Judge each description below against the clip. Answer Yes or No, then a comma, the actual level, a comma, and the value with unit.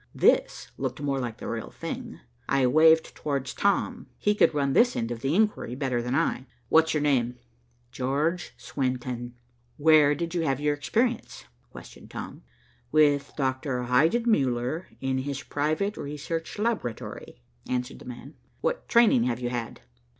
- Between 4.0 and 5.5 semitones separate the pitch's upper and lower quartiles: Yes, average, 4.4 semitones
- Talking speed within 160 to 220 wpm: No, average, 150 wpm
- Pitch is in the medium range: Yes, medium, 145 Hz